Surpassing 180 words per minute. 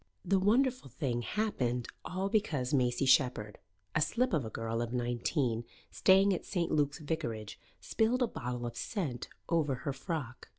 No: average, 160 wpm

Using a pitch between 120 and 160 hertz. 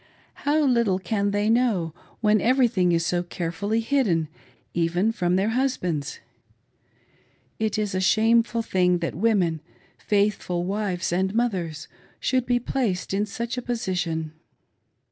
No: high, 200 Hz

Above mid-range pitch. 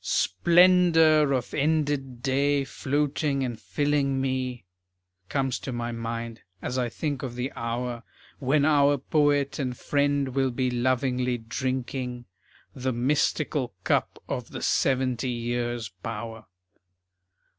No: low, 130 Hz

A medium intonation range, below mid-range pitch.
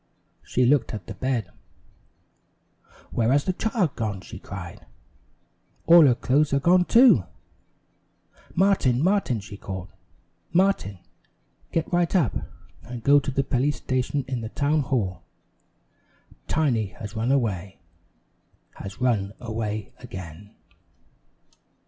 No: wide, 5.9 semitones; low, 125 Hz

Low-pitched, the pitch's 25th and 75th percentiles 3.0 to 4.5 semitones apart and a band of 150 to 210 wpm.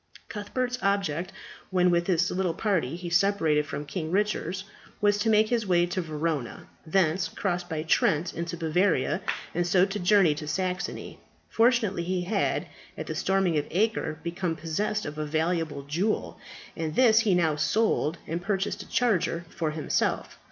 No: medium, 180 Hz; average, 3.7 semitones; average, 165 wpm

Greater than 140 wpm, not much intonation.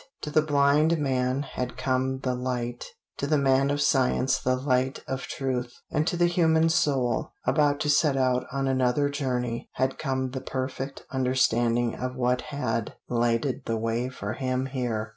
Yes: average, 170 wpm; narrow, 2.2 semitones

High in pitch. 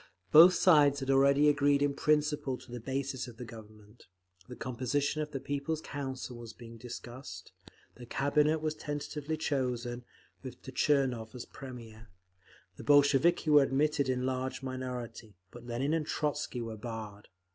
No: low, 135 Hz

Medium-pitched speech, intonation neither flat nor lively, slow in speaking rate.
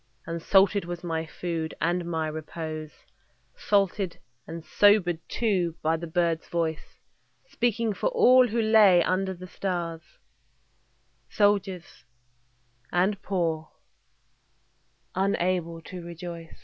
Yes: medium, 175 Hz; average, 3.2 semitones; slow, 110 wpm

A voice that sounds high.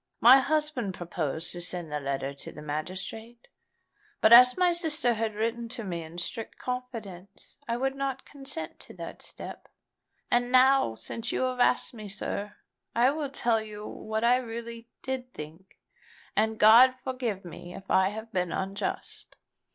Yes: high, 225 Hz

